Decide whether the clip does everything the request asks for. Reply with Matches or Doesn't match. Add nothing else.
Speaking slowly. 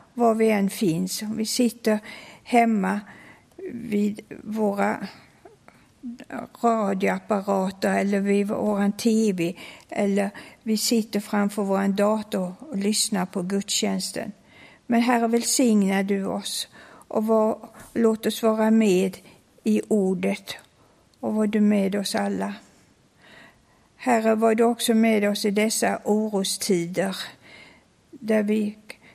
Matches